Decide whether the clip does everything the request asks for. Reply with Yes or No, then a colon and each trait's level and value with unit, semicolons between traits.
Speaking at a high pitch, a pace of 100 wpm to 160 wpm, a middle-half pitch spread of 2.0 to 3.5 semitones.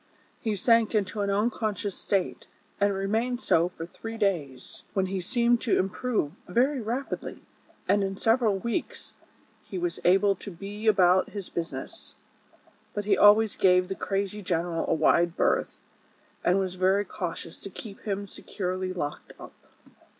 Yes: high, 195 Hz; average, 155 wpm; average, 2.9 semitones